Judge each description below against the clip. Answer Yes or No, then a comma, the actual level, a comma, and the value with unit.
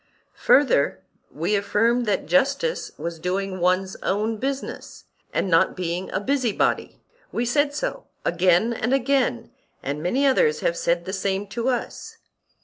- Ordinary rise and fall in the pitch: No, wide, 6.3 semitones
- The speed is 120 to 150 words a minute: Yes, average, 140 wpm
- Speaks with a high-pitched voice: Yes, high, 205 Hz